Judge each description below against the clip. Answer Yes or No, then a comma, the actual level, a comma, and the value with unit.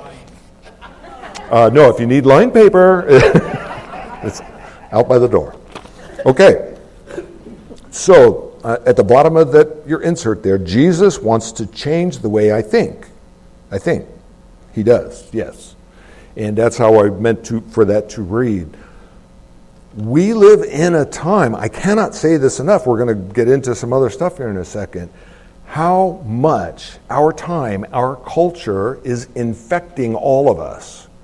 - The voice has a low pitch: Yes, low, 125 Hz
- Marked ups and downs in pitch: Yes, wide, 7.9 semitones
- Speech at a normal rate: Yes, average, 150 wpm